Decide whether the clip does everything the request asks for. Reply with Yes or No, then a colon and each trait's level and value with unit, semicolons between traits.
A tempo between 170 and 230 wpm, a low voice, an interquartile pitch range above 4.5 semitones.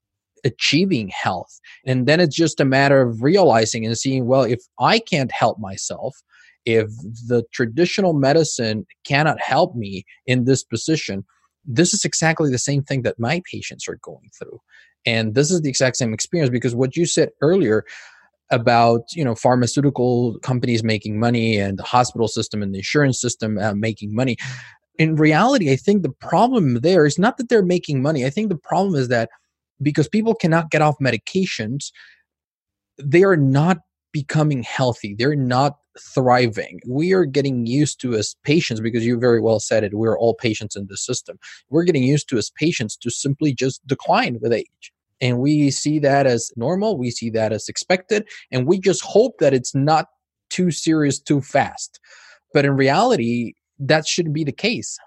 Yes: average, 180 wpm; low, 130 Hz; average, 5.1 semitones